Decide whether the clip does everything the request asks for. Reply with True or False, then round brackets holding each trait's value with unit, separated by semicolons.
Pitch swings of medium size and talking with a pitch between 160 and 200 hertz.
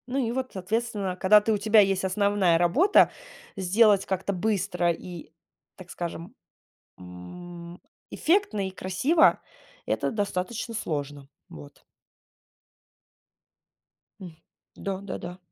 True (3.5 semitones; 190 Hz)